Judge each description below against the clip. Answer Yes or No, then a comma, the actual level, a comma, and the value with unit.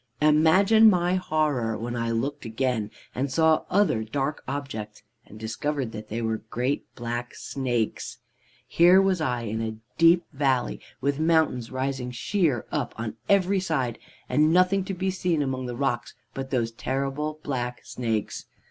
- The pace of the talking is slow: No, average, 155 wpm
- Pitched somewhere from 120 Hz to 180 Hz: Yes, low, 135 Hz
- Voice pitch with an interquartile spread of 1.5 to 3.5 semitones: No, average, 5.3 semitones